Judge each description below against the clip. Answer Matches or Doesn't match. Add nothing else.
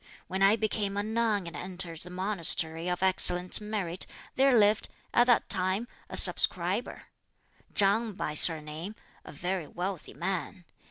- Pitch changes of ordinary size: Matches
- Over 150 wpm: Doesn't match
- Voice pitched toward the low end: Doesn't match